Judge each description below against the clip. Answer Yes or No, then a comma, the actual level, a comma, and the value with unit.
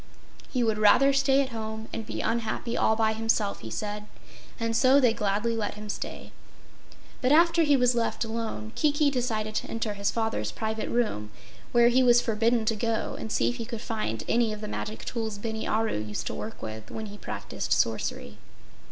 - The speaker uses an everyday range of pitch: No, narrow, 2.1 semitones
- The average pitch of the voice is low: No, high, 225 Hz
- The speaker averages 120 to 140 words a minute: No, average, 195 wpm